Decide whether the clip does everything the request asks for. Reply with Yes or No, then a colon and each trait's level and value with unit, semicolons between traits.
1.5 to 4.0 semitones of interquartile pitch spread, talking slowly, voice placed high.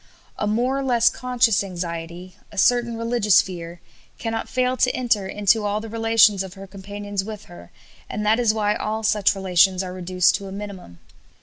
No: average, 3.2 semitones; average, 185 wpm; high, 205 Hz